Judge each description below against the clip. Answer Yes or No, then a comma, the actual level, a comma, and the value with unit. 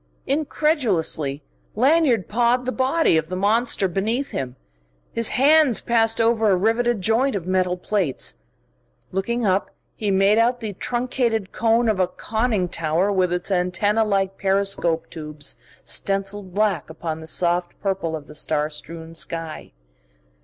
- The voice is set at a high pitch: Yes, high, 200 Hz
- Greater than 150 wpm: No, average, 145 wpm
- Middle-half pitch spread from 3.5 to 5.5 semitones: Yes, average, 4.9 semitones